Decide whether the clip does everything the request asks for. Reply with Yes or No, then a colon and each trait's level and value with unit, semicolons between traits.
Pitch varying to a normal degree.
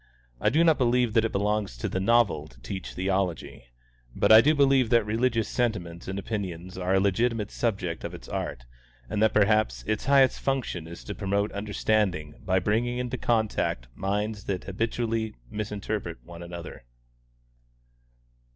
Yes: average, 3.7 semitones